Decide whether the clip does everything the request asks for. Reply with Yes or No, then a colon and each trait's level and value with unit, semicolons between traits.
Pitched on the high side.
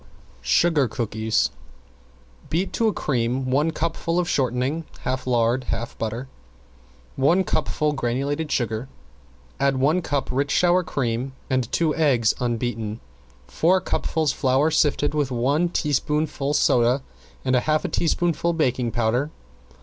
No: low, 135 Hz